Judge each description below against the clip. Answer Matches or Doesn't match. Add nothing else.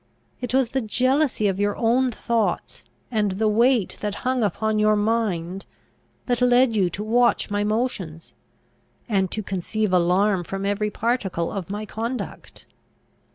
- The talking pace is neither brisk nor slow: Matches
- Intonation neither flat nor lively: Matches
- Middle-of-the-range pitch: Doesn't match